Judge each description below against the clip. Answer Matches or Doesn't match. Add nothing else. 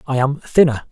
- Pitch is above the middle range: Doesn't match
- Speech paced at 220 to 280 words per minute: Doesn't match